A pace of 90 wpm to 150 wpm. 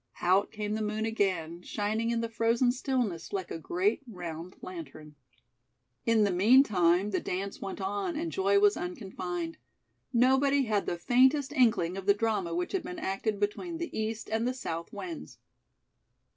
No: average, 165 wpm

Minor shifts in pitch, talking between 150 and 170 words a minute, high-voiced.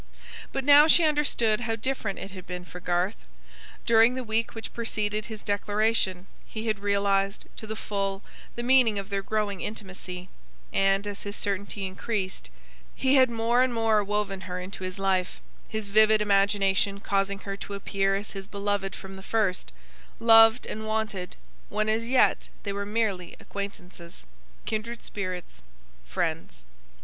Yes: narrow, 2.3 semitones; average, 160 wpm; high, 205 Hz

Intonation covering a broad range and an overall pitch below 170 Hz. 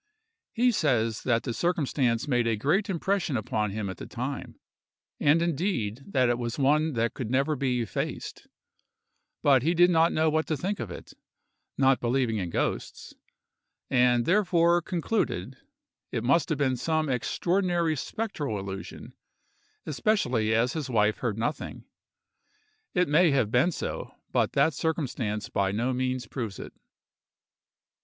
Yes: wide, 5.9 semitones; low, 135 Hz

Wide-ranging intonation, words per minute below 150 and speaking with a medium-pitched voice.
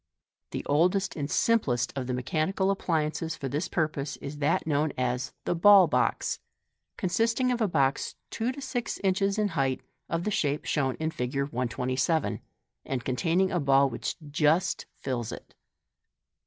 No: wide, 5.8 semitones; average, 160 wpm; medium, 155 Hz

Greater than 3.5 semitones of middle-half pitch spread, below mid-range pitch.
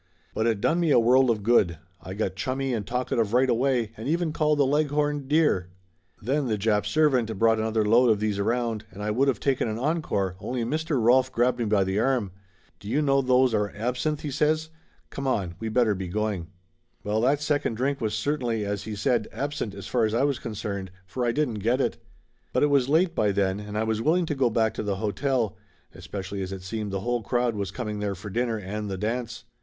Yes: average, 4.4 semitones; low, 115 Hz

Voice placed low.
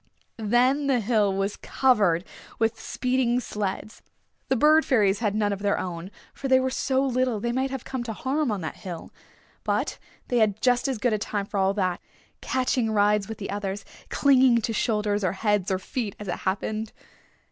No: high, 220 Hz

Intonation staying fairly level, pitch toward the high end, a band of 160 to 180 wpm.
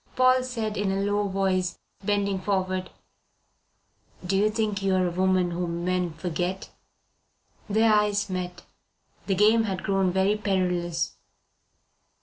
No: narrow, 2.1 semitones; high, 195 Hz; slow, 135 wpm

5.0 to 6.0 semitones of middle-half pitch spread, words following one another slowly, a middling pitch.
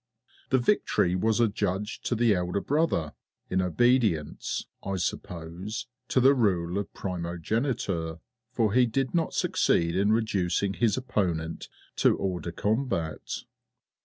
No: average, 5.3 semitones; slow, 130 wpm; low, 100 Hz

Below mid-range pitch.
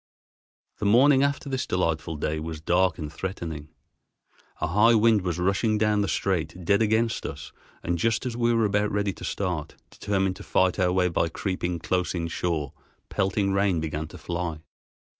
Yes: very low, 95 Hz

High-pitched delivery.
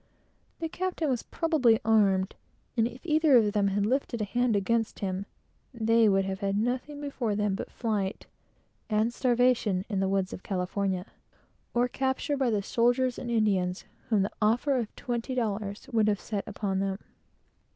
Yes: high, 220 Hz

